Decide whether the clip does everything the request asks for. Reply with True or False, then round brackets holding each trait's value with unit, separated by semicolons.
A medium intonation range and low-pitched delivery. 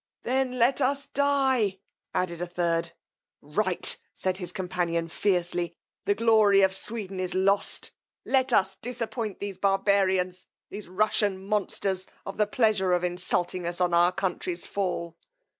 False (3.1 semitones; 190 Hz)